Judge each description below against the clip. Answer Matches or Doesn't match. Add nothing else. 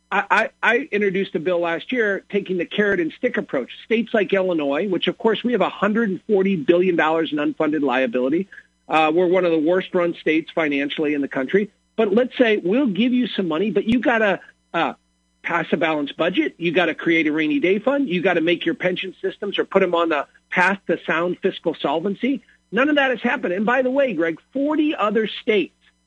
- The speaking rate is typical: Doesn't match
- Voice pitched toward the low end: Doesn't match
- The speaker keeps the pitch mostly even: Doesn't match